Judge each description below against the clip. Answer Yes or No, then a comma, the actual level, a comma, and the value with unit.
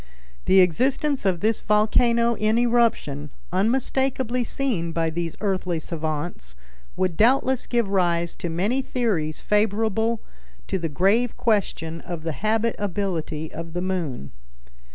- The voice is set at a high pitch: Yes, high, 195 Hz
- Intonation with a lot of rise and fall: Yes, wide, 5.7 semitones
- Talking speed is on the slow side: Yes, slow, 125 wpm